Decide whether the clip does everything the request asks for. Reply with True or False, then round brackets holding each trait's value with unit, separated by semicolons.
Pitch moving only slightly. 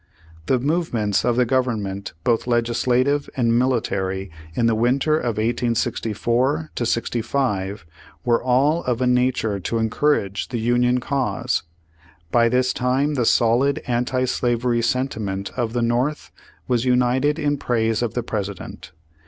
True (2.1 semitones)